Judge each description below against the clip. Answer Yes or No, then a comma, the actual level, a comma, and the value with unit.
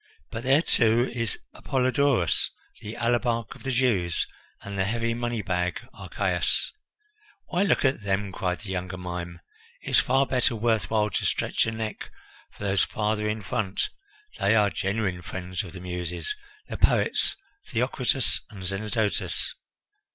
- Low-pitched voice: Yes, low, 110 Hz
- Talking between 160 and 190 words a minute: No, average, 150 wpm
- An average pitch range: Yes, average, 4.4 semitones